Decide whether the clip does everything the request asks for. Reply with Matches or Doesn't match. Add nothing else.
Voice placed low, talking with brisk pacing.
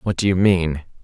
Matches